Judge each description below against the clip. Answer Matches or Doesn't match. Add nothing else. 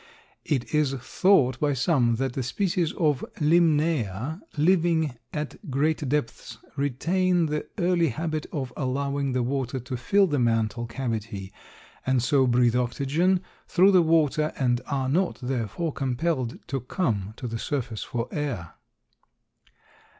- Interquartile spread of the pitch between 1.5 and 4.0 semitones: Doesn't match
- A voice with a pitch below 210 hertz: Matches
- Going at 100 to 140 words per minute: Matches